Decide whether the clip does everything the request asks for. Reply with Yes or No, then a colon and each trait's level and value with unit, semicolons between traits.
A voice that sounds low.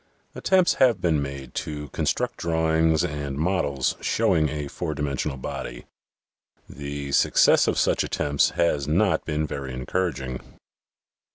Yes: very low, 75 Hz